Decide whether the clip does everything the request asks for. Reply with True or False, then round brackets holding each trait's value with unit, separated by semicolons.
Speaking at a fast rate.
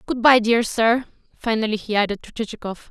False (185 wpm)